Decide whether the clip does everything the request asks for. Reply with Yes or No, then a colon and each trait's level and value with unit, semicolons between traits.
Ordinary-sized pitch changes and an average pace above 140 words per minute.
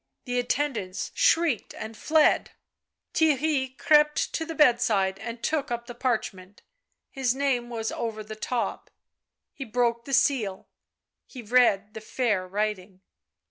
No: average, 3.9 semitones; slow, 135 wpm